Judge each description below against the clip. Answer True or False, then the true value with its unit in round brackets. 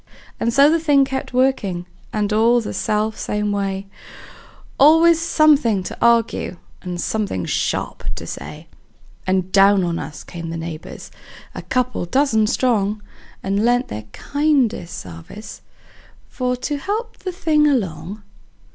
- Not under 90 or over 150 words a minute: True (140 wpm)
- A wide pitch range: True (6.1 semitones)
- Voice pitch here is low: False (220 Hz)